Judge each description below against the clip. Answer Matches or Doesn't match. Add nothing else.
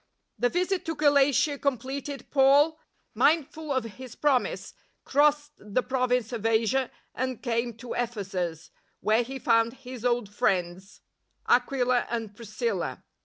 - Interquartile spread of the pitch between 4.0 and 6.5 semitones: Doesn't match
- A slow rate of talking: Matches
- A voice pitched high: Matches